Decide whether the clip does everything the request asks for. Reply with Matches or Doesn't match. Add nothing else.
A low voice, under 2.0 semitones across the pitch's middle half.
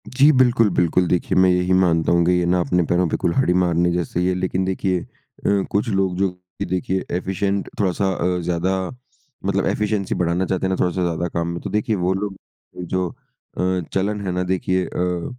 Matches